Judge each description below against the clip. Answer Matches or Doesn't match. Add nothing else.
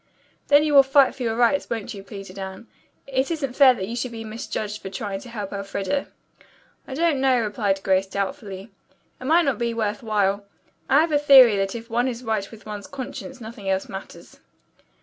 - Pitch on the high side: Matches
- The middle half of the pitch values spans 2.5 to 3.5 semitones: Doesn't match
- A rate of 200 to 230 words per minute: Matches